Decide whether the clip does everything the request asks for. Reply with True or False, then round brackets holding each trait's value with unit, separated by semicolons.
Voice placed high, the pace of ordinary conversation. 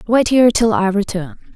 True (220 Hz; 195 wpm)